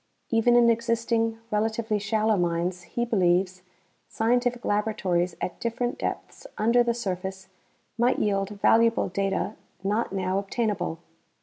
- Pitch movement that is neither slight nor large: Yes, average, 3.4 semitones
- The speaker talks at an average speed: No, slow, 120 wpm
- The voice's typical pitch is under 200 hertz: No, high, 215 Hz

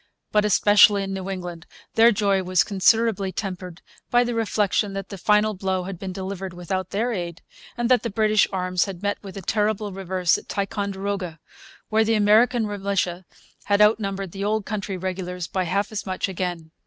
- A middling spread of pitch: No, narrow, 2.2 semitones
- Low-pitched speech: No, high, 195 Hz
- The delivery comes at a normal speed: Yes, average, 180 wpm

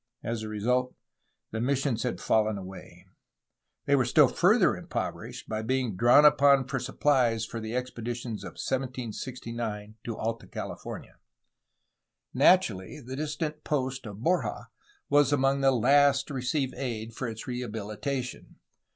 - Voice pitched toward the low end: Yes, low, 125 Hz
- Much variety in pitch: No, average, 3.5 semitones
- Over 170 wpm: No, average, 140 wpm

